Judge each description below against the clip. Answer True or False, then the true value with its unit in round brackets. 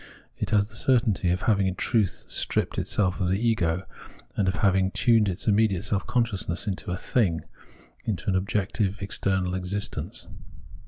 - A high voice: False (100 Hz)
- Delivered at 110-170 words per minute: True (165 wpm)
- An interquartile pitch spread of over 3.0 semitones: False (2.5 semitones)